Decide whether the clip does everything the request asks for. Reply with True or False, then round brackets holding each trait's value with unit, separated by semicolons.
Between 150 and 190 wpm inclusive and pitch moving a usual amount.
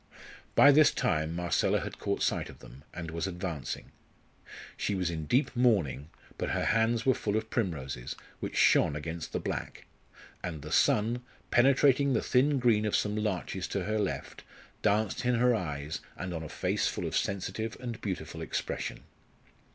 False (170 wpm; 6.4 semitones)